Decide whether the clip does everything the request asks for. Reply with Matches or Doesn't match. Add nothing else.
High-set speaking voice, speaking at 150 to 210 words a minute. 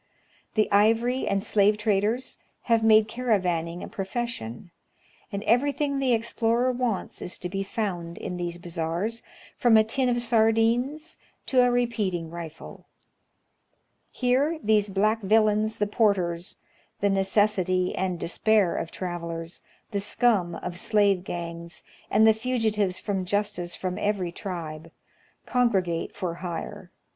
Doesn't match